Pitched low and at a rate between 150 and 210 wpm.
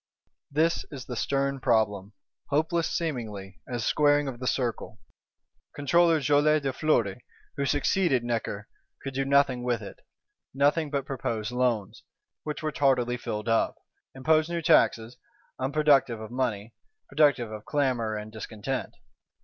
No: low, 130 Hz; slow, 135 wpm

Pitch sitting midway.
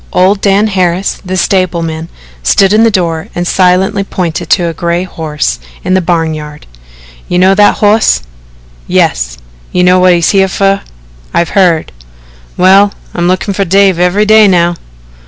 Yes: medium, 180 Hz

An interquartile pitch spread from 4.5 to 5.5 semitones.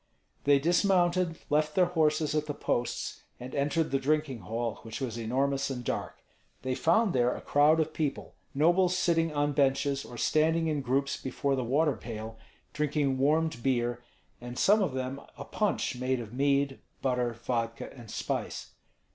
No: average, 3.8 semitones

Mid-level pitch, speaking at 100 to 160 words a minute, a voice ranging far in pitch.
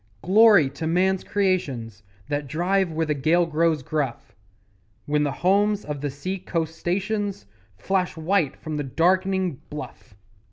No: medium, 165 Hz; average, 145 wpm; average, 4.3 semitones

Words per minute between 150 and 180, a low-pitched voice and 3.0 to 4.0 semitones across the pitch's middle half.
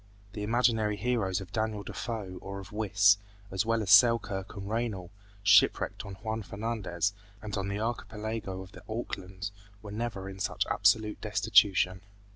No: average, 155 wpm; low, 105 Hz; narrow, 2.4 semitones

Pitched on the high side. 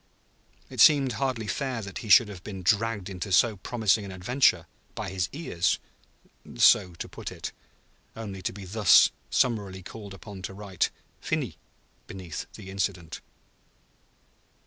No: low, 100 Hz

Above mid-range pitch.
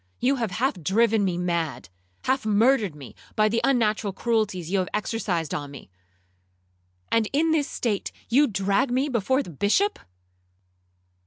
Yes: high, 200 Hz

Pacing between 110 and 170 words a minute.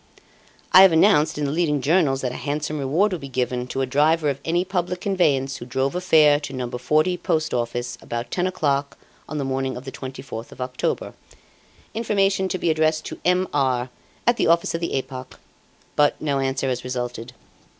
No: average, 200 wpm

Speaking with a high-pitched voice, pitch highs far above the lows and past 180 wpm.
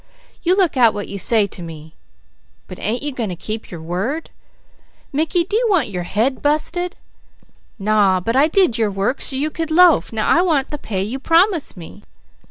Yes: very high, 255 Hz; wide, 8.2 semitones; average, 200 wpm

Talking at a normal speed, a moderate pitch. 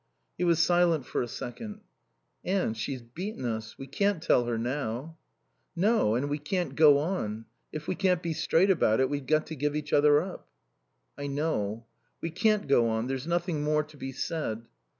Yes: average, 190 wpm; medium, 150 Hz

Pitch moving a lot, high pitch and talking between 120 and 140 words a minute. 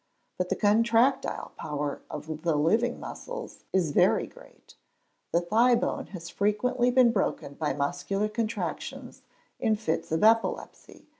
Yes: wide, 6.1 semitones; high, 210 Hz; slow, 135 wpm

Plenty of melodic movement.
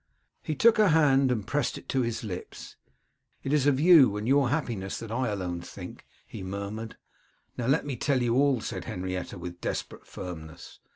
Yes: wide, 6.3 semitones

